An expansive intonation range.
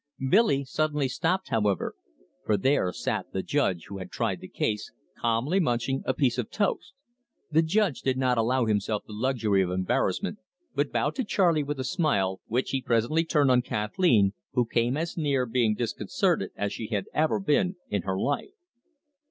Yes: wide, 6.3 semitones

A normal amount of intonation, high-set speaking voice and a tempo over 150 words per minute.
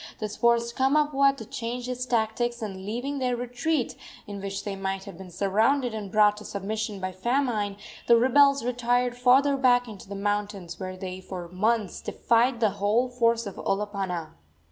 Yes: average, 3.8 semitones; high, 225 Hz; average, 170 wpm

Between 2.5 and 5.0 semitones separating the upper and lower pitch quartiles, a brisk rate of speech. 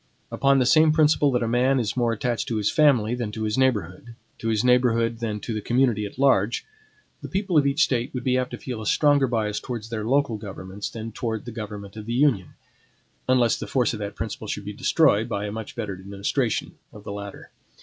Yes: average, 3.5 semitones; fast, 225 wpm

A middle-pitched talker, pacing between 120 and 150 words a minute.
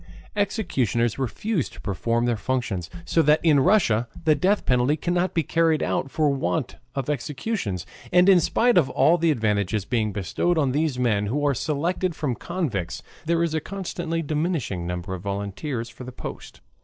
No: medium, 145 Hz; average, 170 wpm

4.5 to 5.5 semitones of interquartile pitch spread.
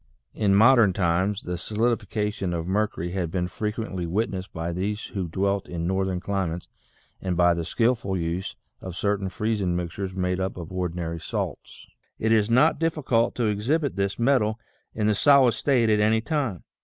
No: average, 3.8 semitones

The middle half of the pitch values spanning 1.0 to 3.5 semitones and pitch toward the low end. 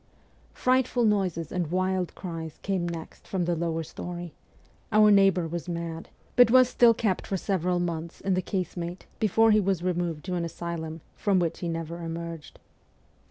No: narrow, 2.6 semitones; medium, 175 Hz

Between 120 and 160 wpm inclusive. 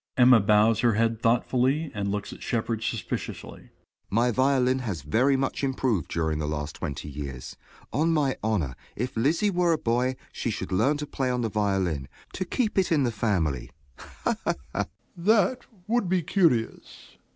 No: average, 185 wpm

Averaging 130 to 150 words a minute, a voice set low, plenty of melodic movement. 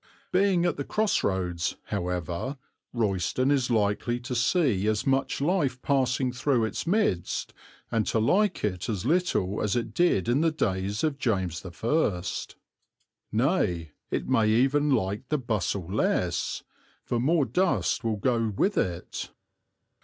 Yes: average, 145 wpm; low, 120 Hz; wide, 6.5 semitones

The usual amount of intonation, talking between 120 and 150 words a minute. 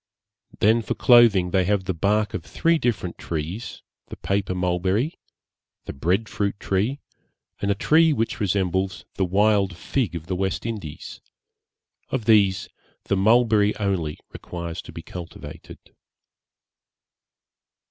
Yes: average, 3.5 semitones; slow, 135 wpm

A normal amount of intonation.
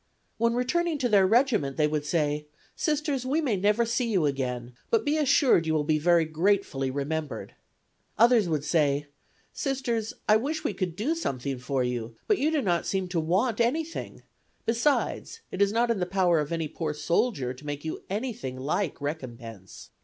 No: wide, 8.5 semitones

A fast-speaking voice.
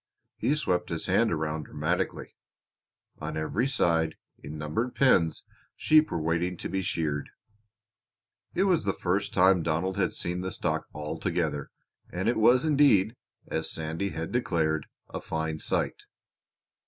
No: average, 145 wpm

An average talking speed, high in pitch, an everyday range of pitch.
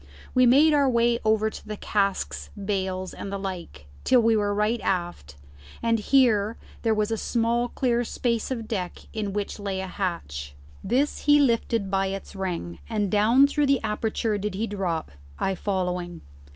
Yes: average, 170 wpm; high, 210 Hz; average, 3.6 semitones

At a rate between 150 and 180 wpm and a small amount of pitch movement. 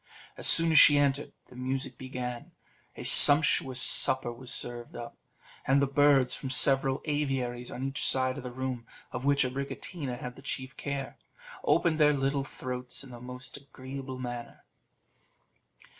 Yes: average, 160 wpm; narrow, 1.9 semitones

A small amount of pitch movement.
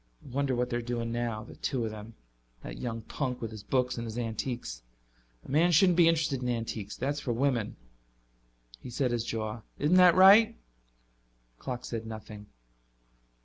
No: average, 3.8 semitones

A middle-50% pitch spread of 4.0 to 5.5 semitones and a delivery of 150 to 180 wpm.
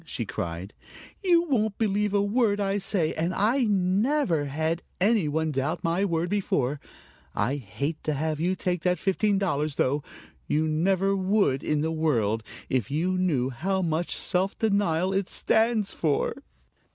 Yes: average, 4.8 semitones; average, 160 wpm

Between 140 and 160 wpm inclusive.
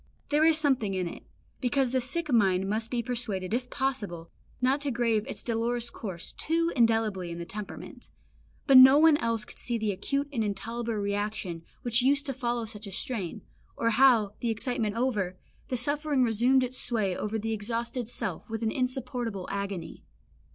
No: average, 180 wpm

